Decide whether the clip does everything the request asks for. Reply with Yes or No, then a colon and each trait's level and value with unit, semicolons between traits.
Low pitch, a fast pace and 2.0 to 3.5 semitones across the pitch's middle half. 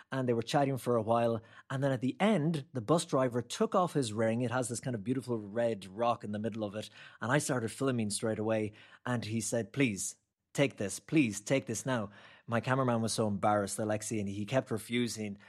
Yes: low, 120 Hz; fast, 225 wpm; average, 3.2 semitones